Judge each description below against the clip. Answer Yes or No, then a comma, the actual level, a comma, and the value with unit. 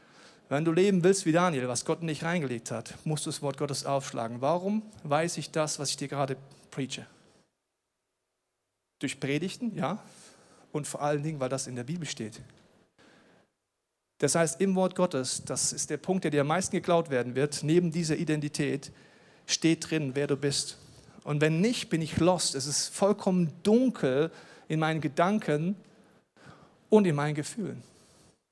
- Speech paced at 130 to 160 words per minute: No, average, 170 wpm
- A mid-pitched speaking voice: Yes, medium, 155 Hz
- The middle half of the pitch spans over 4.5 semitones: No, average, 4.1 semitones